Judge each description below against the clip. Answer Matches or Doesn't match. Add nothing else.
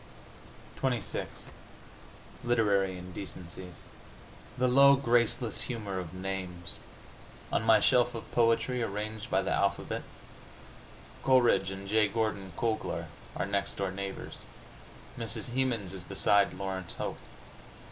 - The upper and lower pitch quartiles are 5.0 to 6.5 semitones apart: Doesn't match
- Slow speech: Matches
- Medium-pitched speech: Doesn't match